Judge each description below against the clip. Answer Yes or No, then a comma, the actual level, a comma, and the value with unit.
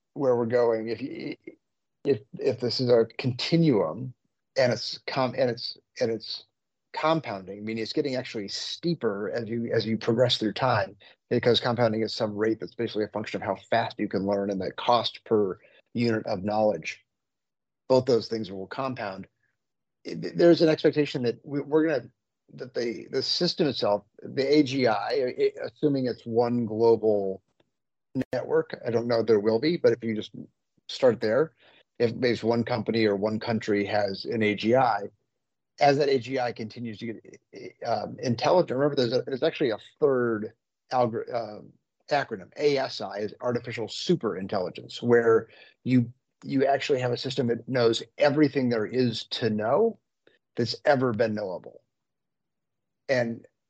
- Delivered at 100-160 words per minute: Yes, average, 155 wpm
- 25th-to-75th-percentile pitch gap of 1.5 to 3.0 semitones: No, average, 3.7 semitones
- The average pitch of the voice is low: Yes, low, 120 Hz